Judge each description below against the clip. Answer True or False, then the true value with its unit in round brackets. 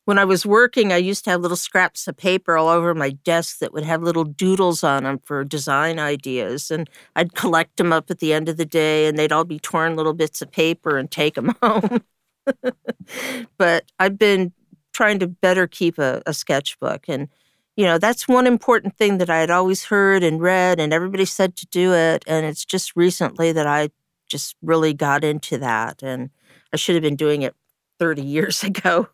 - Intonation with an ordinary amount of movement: True (3.6 semitones)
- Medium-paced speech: False (210 wpm)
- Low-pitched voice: False (170 Hz)